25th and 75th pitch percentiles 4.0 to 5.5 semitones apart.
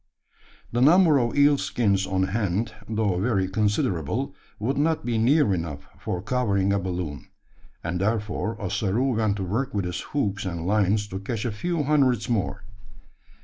Yes: average, 4.6 semitones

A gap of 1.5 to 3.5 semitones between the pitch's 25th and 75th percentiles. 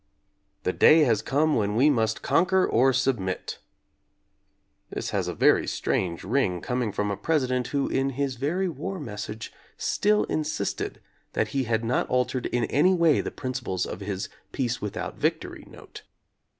No: average, 5.1 semitones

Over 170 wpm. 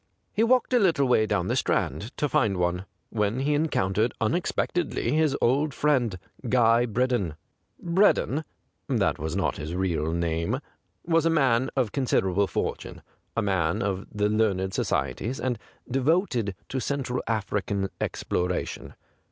No: average, 145 wpm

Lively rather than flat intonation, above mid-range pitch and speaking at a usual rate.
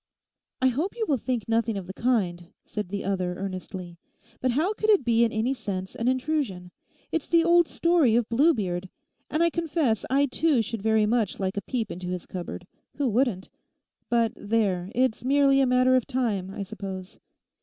Yes: wide, 5.8 semitones; high, 230 Hz; average, 185 wpm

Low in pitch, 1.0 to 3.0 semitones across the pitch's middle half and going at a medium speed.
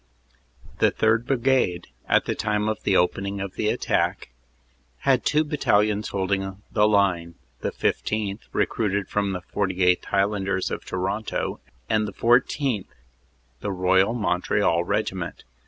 No: low, 100 Hz; narrow, 2.5 semitones; slow, 130 wpm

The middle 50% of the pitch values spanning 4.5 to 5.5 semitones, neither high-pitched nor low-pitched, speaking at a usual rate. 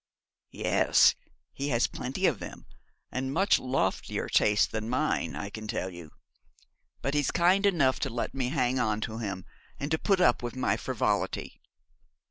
No: average, 5.2 semitones; low, 130 Hz; average, 165 wpm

